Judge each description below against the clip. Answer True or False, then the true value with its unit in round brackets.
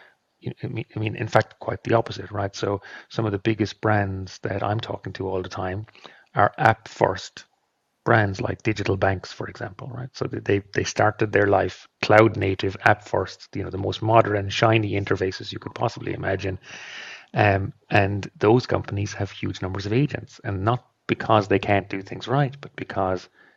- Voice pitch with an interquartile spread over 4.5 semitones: False (2.9 semitones)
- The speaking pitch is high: False (105 Hz)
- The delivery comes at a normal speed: True (180 wpm)